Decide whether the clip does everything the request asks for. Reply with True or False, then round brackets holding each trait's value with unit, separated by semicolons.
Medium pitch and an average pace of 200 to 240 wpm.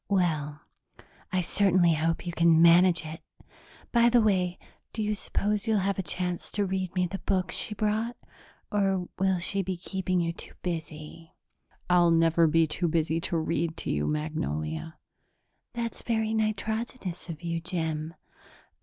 False (180 Hz; 155 wpm)